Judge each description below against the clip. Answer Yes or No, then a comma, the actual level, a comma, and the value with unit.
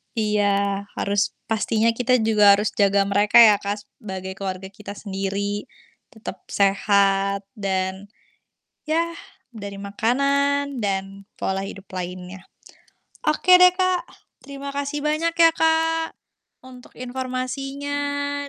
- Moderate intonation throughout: No, wide, 6.1 semitones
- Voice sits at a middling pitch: No, high, 215 Hz